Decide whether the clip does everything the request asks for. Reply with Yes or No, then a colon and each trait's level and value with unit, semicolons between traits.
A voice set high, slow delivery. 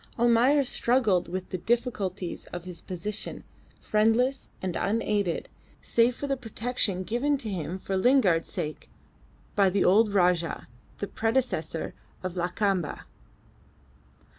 Yes: high, 205 Hz; slow, 120 wpm